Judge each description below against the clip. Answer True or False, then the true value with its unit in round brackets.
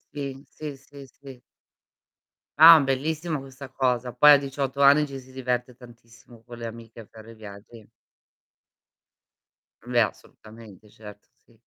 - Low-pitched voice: True (125 Hz)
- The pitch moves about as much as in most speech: True (3.2 semitones)